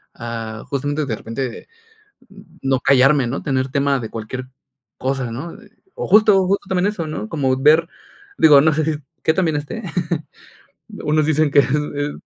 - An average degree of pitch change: Yes, average, 3.3 semitones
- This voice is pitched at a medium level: Yes, medium, 145 Hz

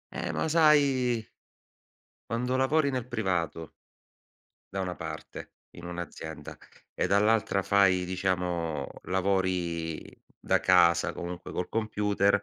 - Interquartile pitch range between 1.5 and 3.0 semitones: No, average, 4.5 semitones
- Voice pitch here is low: Yes, very low, 95 Hz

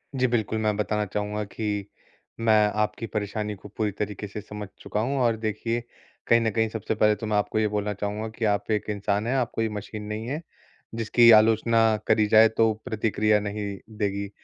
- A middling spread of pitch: No, narrow, 1.4 semitones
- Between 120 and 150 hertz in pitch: No, low, 105 Hz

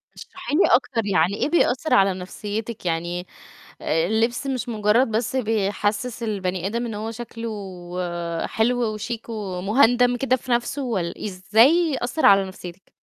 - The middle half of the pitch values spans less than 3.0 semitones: No, average, 3.8 semitones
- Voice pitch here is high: Yes, high, 225 Hz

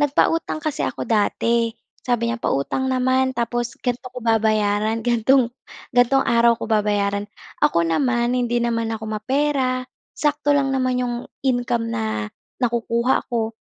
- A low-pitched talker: No, high, 235 Hz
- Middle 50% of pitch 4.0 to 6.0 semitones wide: No, average, 2.8 semitones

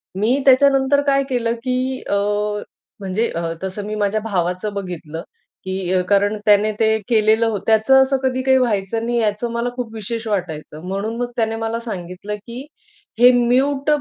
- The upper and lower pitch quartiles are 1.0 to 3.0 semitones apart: No, average, 3.7 semitones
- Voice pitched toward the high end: Yes, high, 220 Hz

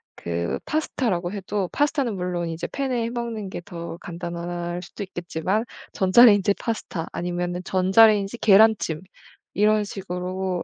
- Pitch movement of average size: Yes, average, 3.7 semitones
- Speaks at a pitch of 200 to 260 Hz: No, high, 190 Hz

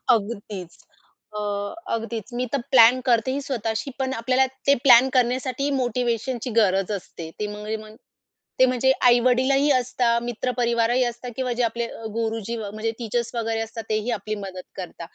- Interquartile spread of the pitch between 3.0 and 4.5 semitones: No, narrow, 2.5 semitones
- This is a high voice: Yes, high, 235 Hz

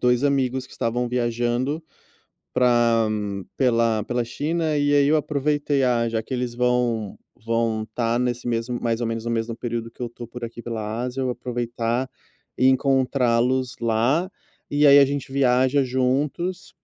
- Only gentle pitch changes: Yes, narrow, 2.3 semitones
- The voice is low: Yes, low, 125 Hz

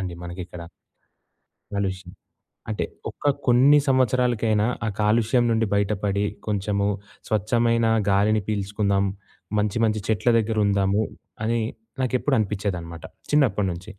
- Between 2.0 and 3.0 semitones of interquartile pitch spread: Yes, average, 2.7 semitones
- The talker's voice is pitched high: No, low, 105 Hz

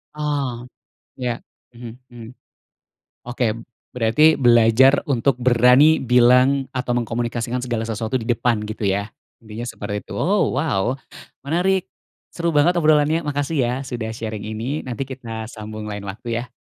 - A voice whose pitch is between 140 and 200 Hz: No, low, 120 Hz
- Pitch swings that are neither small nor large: Yes, average, 3.6 semitones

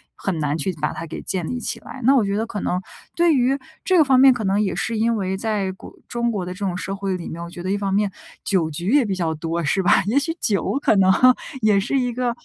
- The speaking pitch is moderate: No, high, 200 Hz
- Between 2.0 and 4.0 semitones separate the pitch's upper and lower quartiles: No, average, 4.6 semitones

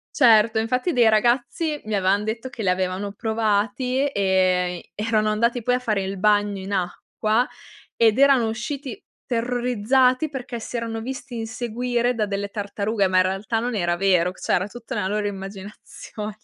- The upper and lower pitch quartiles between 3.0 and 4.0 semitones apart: Yes, average, 3.3 semitones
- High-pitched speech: Yes, high, 220 Hz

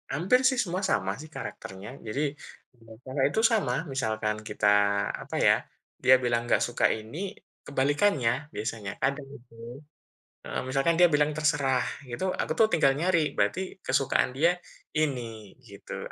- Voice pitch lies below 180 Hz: Yes, low, 135 Hz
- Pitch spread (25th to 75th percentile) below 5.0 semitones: No, average, 5.3 semitones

